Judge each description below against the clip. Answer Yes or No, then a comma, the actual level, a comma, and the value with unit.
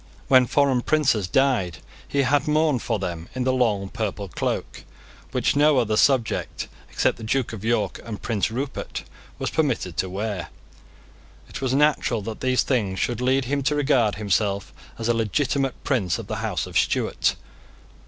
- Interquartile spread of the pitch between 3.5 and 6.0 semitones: Yes, average, 4.6 semitones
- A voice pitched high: No, low, 120 Hz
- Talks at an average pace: Yes, average, 170 wpm